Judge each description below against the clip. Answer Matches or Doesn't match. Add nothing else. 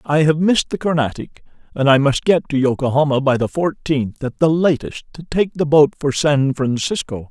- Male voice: Matches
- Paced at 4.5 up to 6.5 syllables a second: Matches